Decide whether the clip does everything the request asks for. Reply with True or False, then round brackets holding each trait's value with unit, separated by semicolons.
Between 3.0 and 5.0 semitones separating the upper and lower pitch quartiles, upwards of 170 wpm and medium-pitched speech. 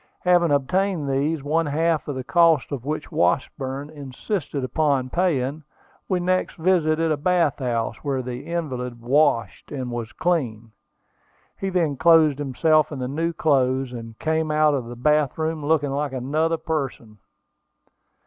False (3.7 semitones; 150 wpm; 145 Hz)